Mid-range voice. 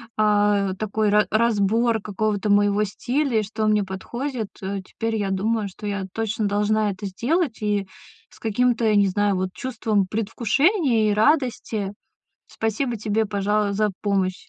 No: high, 210 Hz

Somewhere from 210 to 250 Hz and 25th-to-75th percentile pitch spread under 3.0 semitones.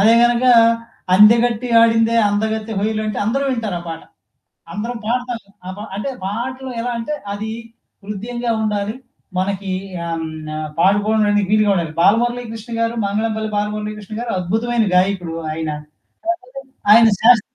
Yes: high, 215 Hz; narrow, 2.6 semitones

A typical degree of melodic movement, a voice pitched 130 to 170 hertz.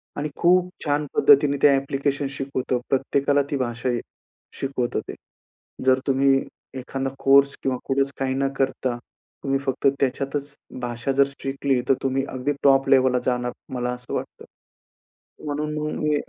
No: narrow, 1.4 semitones; low, 135 Hz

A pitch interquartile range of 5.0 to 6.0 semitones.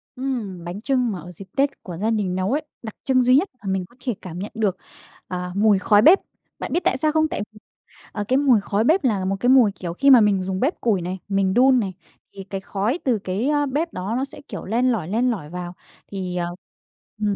Yes: average, 5.3 semitones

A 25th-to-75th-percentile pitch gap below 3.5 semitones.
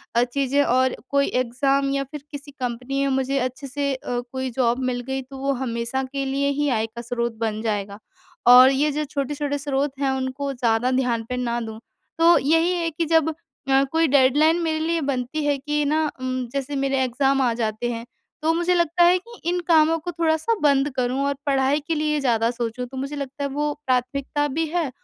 Yes: average, 2.9 semitones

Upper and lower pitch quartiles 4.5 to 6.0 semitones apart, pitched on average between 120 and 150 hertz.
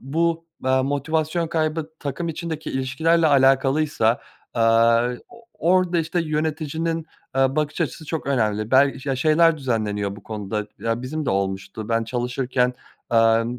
Yes: wide, 5.6 semitones; low, 135 Hz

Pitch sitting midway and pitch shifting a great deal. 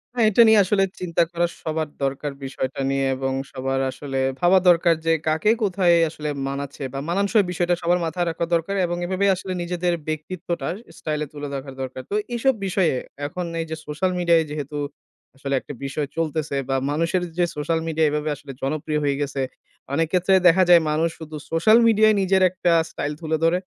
No: medium, 165 Hz; average, 3.6 semitones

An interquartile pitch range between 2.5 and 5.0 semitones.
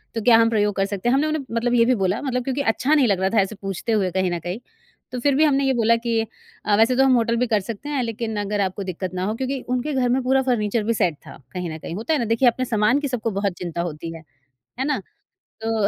Yes: average, 4.6 semitones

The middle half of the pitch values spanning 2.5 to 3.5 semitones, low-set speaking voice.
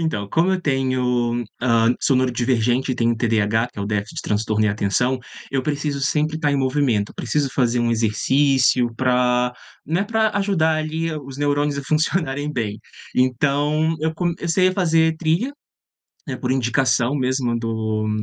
No: average, 4.5 semitones; low, 130 Hz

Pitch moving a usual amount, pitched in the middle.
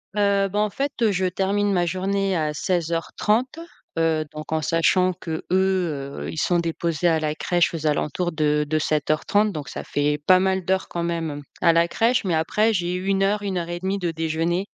Yes: average, 3.4 semitones; medium, 175 Hz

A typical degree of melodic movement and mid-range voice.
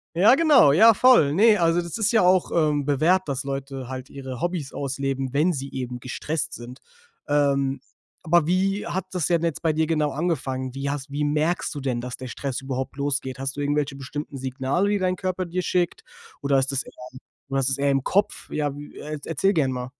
Yes: average, 4.4 semitones; medium, 145 Hz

